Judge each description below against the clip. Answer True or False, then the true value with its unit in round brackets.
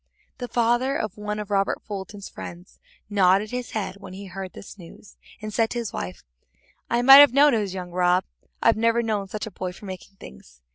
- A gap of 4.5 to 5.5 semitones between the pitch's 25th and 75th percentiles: False (3.5 semitones)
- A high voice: True (205 Hz)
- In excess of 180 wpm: True (205 wpm)